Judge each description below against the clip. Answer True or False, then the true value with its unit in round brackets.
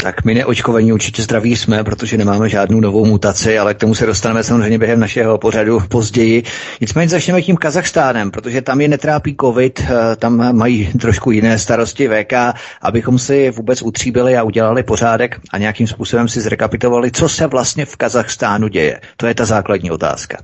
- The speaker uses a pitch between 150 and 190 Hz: False (115 Hz)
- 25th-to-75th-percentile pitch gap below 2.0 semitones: False (2.3 semitones)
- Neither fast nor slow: False (175 wpm)